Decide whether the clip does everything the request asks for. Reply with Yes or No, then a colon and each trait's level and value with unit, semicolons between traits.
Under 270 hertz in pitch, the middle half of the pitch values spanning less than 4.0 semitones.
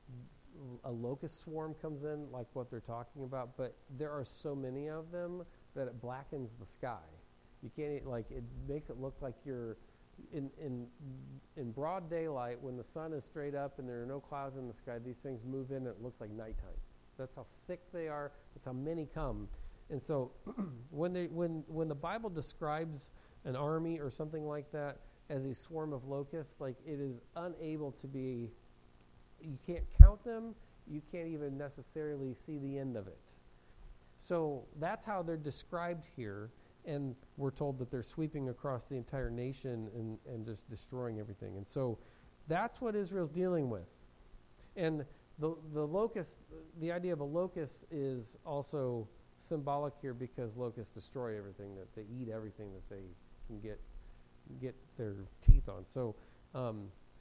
No: low, 135 Hz; average, 4.6 semitones